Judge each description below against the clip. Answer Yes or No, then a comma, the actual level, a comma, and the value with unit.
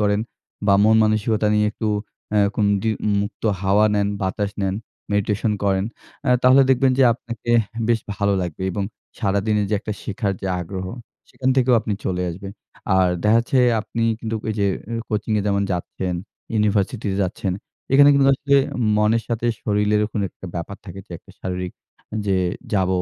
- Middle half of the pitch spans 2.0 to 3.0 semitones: Yes, narrow, 2.5 semitones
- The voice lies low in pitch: Yes, low, 105 Hz